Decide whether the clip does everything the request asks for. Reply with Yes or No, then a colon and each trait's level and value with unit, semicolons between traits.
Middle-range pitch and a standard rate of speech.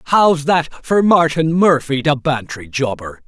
Yes: medium, 145 Hz; average, 145 wpm